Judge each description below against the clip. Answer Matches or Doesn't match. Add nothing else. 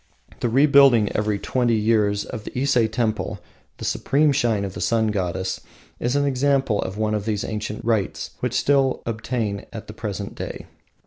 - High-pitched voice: Doesn't match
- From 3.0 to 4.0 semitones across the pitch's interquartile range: Matches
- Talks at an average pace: Matches